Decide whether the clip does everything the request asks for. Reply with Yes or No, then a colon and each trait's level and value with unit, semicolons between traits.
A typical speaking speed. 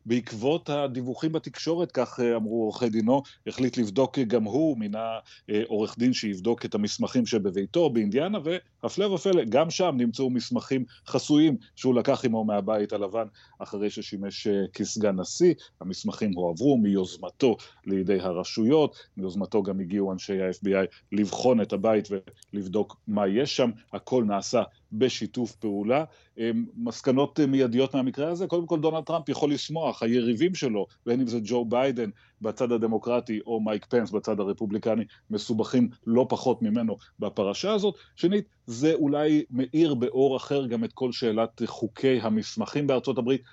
Yes: average, 140 wpm